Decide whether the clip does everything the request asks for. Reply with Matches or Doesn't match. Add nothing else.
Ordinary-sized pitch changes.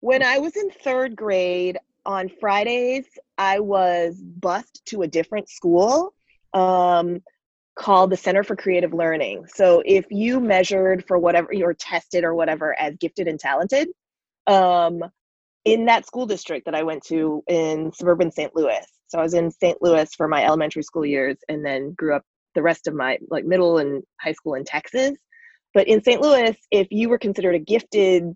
Matches